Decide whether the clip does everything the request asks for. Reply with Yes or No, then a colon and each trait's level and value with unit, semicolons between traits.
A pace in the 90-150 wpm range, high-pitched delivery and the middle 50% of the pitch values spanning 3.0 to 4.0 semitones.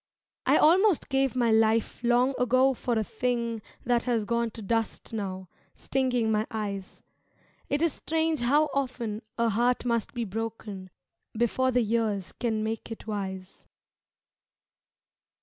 No: average, 140 wpm; high, 235 Hz; narrow, 2.5 semitones